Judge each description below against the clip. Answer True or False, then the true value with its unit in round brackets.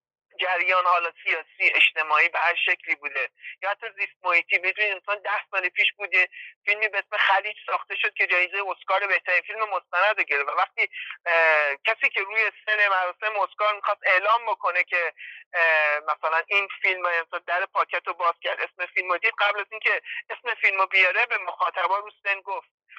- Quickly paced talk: True (175 wpm)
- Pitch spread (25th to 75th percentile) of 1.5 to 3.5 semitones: True (2.9 semitones)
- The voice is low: False (195 Hz)